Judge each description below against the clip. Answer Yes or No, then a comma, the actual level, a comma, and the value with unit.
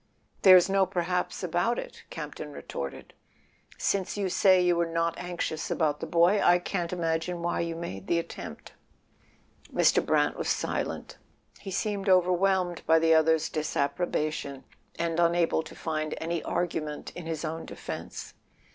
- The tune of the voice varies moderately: No, narrow, 1.9 semitones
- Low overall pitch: No, medium, 170 Hz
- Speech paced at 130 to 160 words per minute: Yes, average, 145 wpm